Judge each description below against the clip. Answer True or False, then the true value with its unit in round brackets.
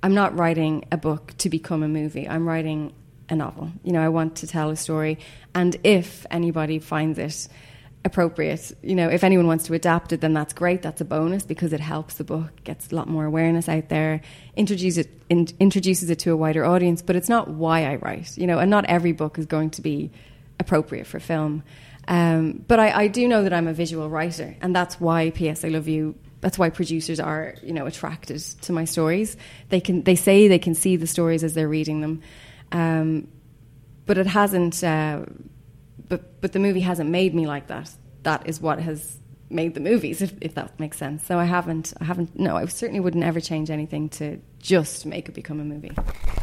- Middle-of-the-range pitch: True (160 Hz)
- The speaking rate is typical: False (215 wpm)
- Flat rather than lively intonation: True (2.3 semitones)